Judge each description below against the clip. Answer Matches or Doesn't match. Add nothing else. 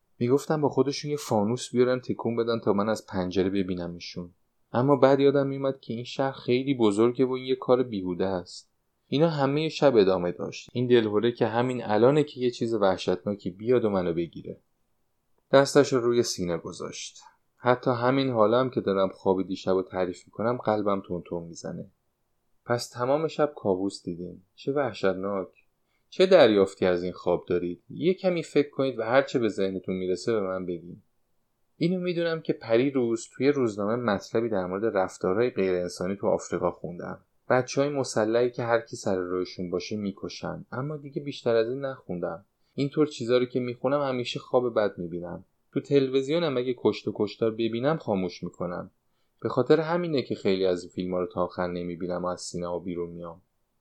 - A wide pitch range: Matches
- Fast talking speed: Matches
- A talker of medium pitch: Doesn't match